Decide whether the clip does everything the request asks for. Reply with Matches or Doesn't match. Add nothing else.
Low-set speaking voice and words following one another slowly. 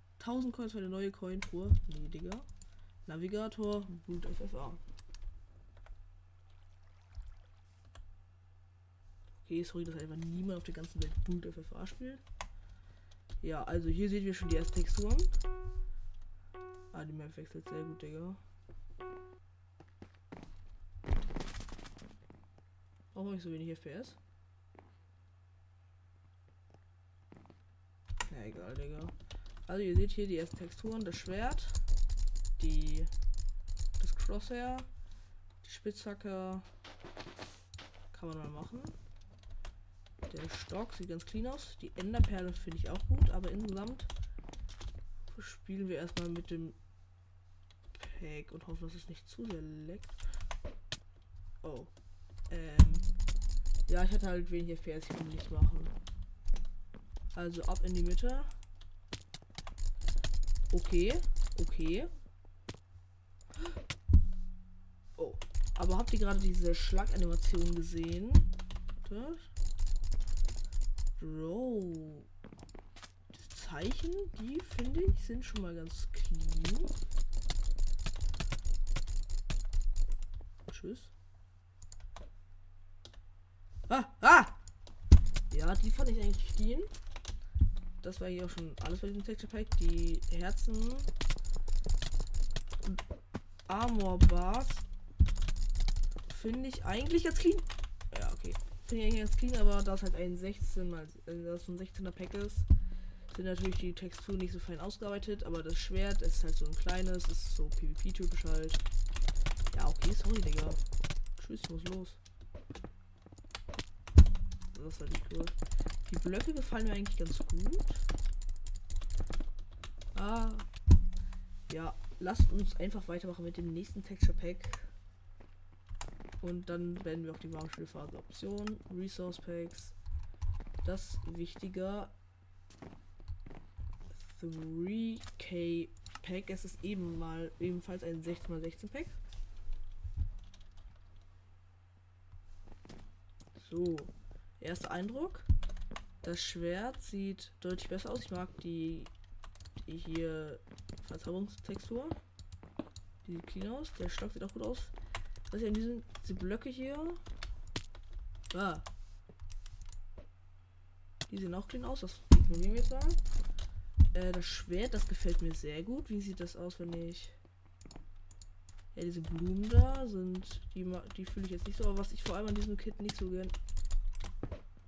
Matches